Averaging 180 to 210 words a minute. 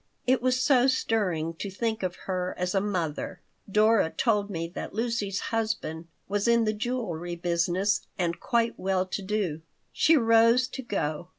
No: average, 165 wpm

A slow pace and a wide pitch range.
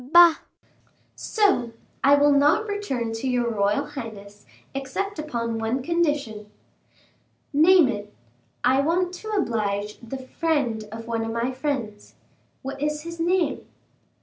Yes: slow, 125 wpm; wide, 6.1 semitones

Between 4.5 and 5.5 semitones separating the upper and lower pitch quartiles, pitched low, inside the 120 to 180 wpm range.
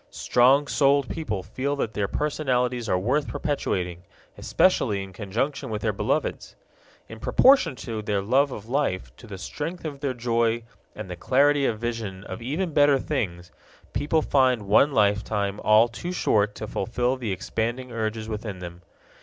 Yes: average, 5.1 semitones; low, 115 Hz; average, 160 wpm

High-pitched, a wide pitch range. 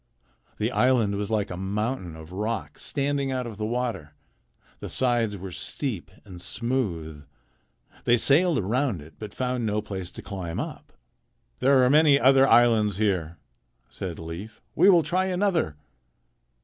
No: low, 110 Hz; wide, 5.9 semitones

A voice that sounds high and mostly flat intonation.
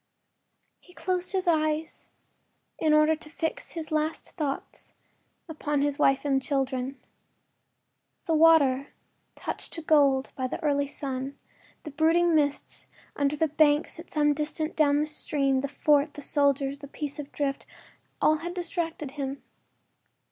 Yes: very high, 295 Hz; narrow, 2.2 semitones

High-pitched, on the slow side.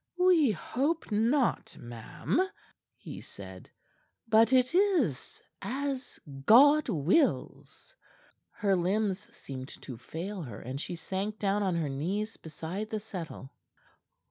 Yes: high, 205 Hz; slow, 115 wpm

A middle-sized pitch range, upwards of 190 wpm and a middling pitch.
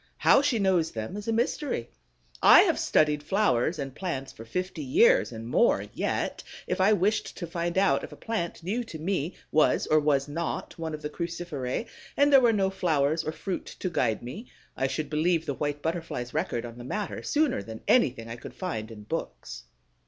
No: wide, 6.2 semitones; average, 200 wpm; medium, 165 Hz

